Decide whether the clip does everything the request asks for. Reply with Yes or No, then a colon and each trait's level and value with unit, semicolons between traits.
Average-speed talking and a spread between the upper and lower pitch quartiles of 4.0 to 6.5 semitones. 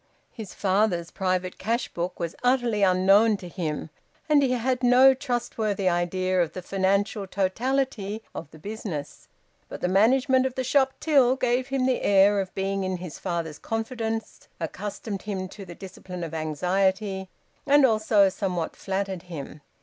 Yes: average, 155 wpm; average, 4.7 semitones